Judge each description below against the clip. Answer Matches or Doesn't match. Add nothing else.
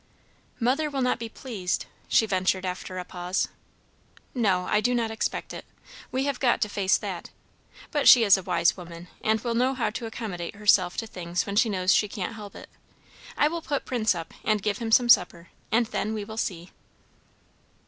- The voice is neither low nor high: Doesn't match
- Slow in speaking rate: Doesn't match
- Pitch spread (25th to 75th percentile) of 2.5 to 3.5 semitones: Doesn't match